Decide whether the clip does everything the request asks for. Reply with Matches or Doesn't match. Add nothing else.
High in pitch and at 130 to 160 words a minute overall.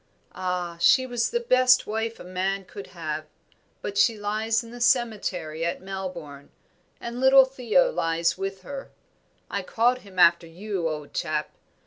Matches